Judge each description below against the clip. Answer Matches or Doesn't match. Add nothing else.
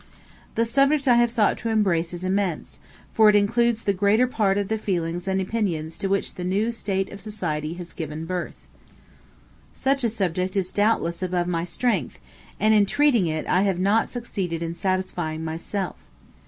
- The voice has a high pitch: Matches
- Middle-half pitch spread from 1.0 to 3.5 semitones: Doesn't match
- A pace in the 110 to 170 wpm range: Doesn't match